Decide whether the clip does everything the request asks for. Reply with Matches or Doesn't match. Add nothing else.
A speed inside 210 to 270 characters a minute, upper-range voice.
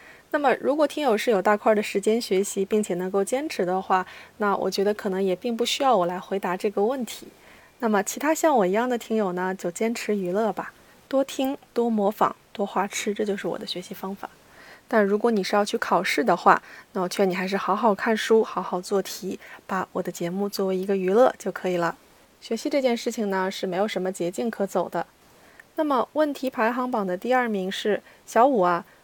Doesn't match